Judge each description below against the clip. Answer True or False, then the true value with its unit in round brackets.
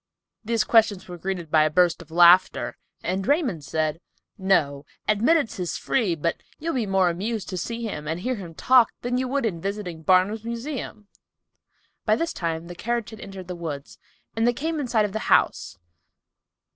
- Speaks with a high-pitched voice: True (195 Hz)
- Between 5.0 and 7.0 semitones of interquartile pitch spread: True (5.4 semitones)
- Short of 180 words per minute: False (185 wpm)